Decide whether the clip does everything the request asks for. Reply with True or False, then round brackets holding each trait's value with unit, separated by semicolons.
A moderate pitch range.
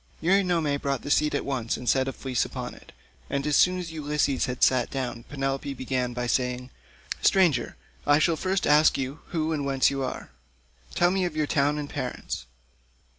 True (3.2 semitones)